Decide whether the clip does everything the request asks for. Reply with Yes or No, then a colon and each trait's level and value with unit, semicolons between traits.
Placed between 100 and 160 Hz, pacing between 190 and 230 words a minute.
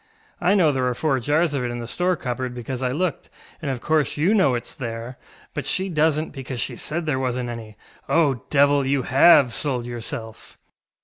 Yes: low, 135 Hz; average, 200 wpm